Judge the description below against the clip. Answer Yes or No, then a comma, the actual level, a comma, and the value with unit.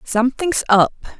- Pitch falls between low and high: No, high, 245 Hz